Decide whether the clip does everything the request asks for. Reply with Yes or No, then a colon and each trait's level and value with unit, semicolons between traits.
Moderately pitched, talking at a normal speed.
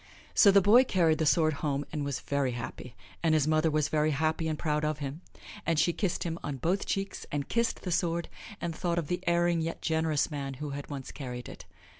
No: medium, 155 Hz; fast, 225 wpm